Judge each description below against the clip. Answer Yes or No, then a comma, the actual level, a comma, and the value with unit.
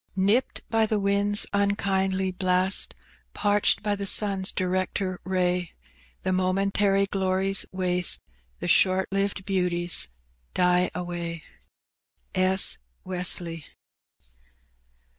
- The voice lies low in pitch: No, high, 190 Hz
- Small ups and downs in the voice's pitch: Yes, narrow, 1.6 semitones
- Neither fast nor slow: No, slow, 95 wpm